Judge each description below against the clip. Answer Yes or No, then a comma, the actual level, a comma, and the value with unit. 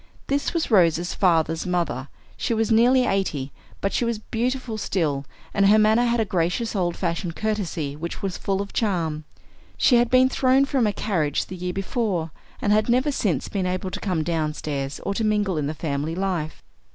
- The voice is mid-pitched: No, high, 195 Hz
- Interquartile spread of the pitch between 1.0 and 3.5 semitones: No, average, 5.3 semitones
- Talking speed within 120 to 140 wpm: No, average, 190 wpm